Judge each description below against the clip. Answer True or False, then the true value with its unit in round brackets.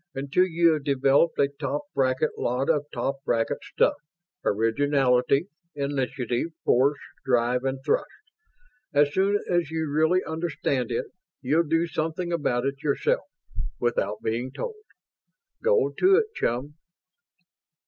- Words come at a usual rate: False (130 wpm)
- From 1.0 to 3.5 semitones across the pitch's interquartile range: False (4.0 semitones)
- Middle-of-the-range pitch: True (145 Hz)